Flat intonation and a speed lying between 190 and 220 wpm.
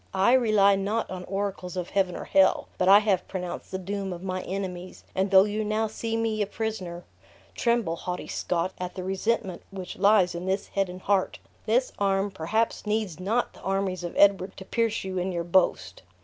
Yes: narrow, 2.3 semitones; average, 200 wpm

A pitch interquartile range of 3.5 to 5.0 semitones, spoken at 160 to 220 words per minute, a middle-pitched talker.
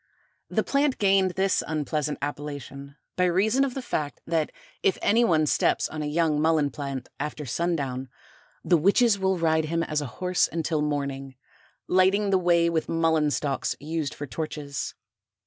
Yes: average, 3.9 semitones; average, 165 wpm; medium, 160 Hz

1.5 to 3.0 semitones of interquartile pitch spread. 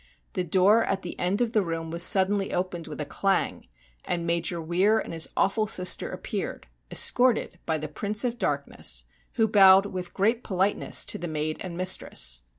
No: average, 3.4 semitones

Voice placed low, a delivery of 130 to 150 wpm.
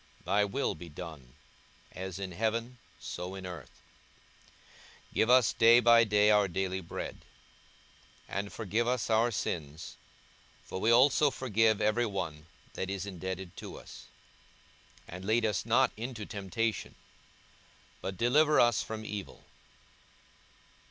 Yes: low, 105 Hz; slow, 135 wpm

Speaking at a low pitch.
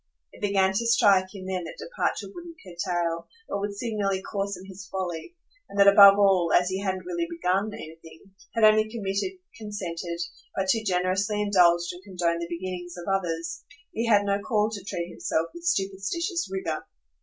No: high, 195 Hz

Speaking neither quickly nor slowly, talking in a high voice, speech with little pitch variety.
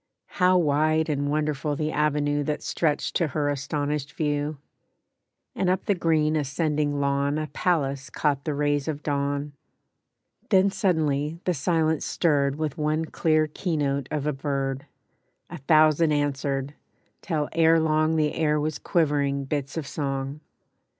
No: average, 145 wpm; medium, 150 Hz; narrow, 1.8 semitones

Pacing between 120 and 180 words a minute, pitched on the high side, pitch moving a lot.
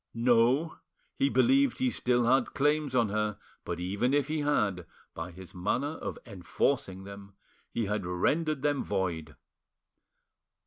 No: average, 140 wpm; low, 115 Hz; wide, 7.3 semitones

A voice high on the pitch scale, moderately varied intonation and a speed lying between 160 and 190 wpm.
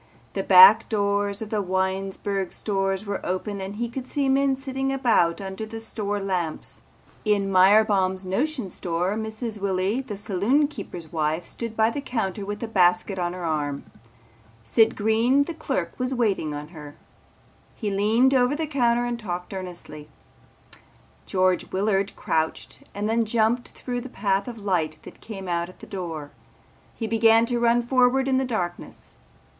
Yes: high, 205 Hz; average, 4.2 semitones; average, 165 wpm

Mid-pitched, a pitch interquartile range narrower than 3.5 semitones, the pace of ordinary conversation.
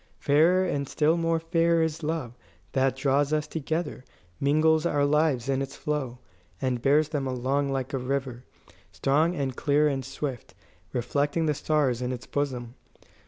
Yes: medium, 145 Hz; average, 2.8 semitones; average, 160 wpm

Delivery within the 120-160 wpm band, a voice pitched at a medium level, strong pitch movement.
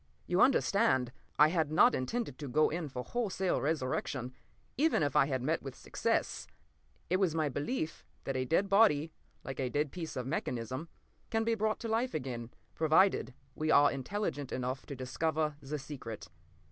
No: average, 170 wpm; medium, 150 Hz; wide, 6.1 semitones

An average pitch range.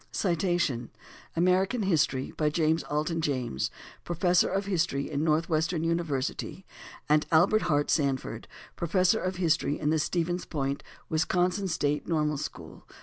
Yes: average, 3.1 semitones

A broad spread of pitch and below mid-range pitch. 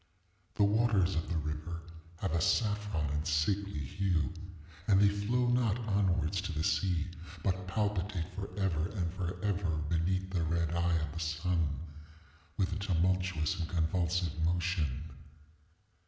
No: average, 3.3 semitones; very low, 90 Hz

